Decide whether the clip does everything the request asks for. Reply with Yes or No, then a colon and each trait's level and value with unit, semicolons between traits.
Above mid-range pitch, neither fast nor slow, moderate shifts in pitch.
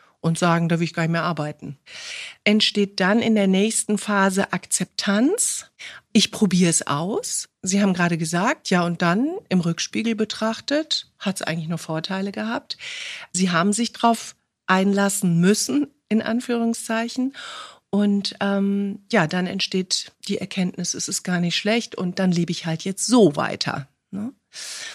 Yes: high, 200 Hz; average, 155 wpm; average, 4.0 semitones